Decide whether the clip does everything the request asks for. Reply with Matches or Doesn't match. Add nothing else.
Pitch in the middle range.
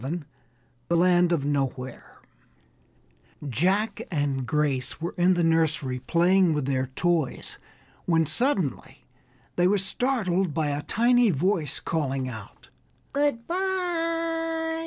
Matches